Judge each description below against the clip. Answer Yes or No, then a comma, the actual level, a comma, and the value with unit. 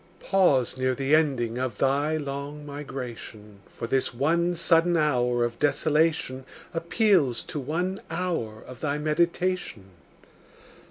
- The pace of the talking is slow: Yes, slow, 120 wpm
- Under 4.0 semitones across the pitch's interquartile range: No, average, 4.5 semitones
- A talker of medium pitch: Yes, medium, 145 Hz